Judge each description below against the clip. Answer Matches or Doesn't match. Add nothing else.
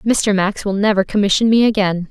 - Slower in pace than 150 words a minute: Doesn't match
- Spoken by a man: Doesn't match